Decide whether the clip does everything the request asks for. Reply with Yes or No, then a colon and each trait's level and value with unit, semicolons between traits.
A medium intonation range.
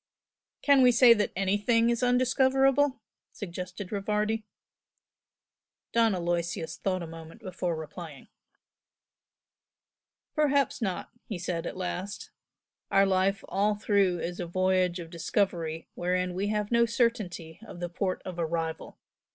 Yes: average, 4.4 semitones